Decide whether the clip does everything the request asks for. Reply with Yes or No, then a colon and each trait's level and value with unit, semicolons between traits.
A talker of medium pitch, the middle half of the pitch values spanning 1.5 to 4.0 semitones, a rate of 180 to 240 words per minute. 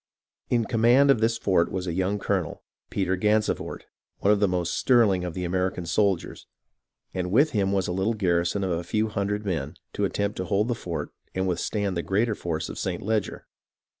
No: very low, 95 Hz; average, 3.0 semitones; average, 200 wpm